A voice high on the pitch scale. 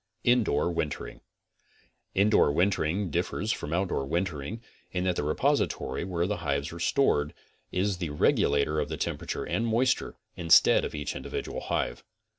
No: very low, 85 Hz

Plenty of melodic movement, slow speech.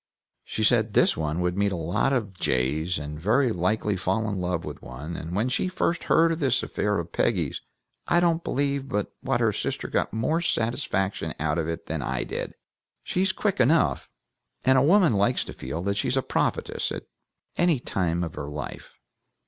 No: wide, 8.2 semitones; average, 195 wpm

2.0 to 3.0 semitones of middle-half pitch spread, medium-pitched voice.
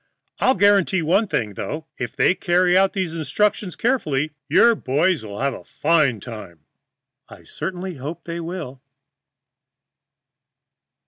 No: wide, 5.6 semitones; medium, 165 Hz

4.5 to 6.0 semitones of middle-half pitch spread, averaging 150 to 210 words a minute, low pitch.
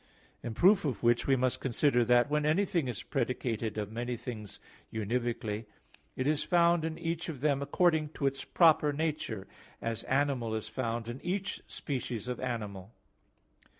Yes: average, 4.9 semitones; average, 160 wpm; low, 130 Hz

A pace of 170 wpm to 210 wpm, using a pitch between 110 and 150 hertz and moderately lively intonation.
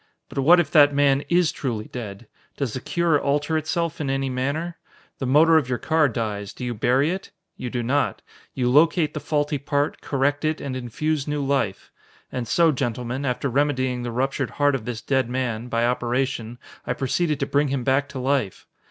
Yes: average, 195 wpm; low, 135 Hz; average, 3.0 semitones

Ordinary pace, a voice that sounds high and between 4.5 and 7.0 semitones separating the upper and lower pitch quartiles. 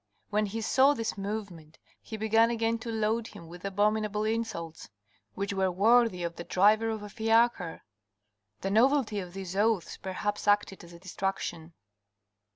No: average, 160 wpm; high, 210 Hz; average, 3.0 semitones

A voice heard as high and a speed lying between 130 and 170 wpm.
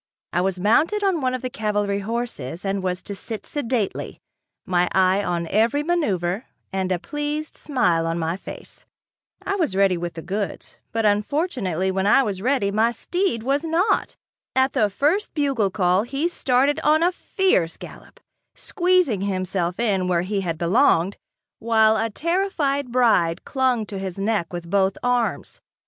Yes: high, 215 Hz; average, 165 wpm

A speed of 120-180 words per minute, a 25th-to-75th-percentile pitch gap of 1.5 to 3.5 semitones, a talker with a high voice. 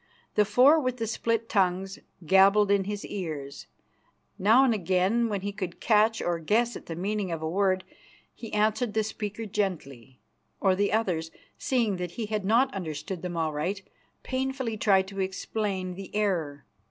Yes: average, 165 wpm; average, 3.2 semitones; high, 200 Hz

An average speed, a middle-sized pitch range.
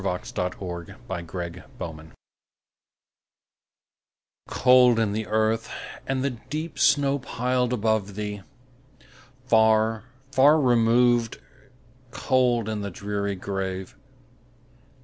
No: slow, 90 wpm; average, 4.0 semitones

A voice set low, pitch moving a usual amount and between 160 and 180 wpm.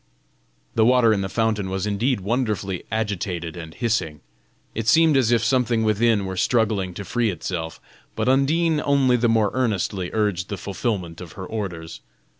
Yes: low, 105 Hz; average, 4.1 semitones; average, 165 wpm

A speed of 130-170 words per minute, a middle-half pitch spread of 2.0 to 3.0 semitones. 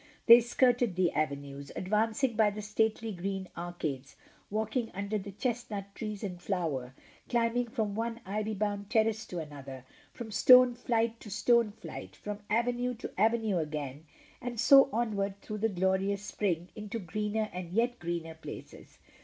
No: average, 155 wpm; average, 4.1 semitones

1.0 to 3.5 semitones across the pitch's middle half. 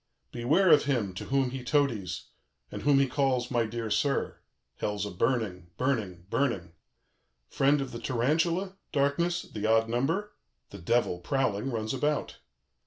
No: average, 4.5 semitones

